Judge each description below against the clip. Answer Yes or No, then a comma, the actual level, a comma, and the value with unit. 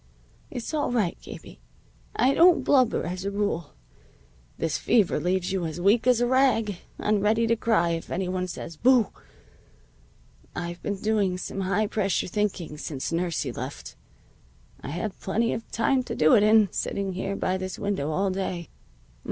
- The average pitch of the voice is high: Yes, high, 195 Hz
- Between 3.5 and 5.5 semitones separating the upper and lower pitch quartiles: Yes, average, 3.8 semitones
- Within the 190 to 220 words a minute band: No, average, 165 wpm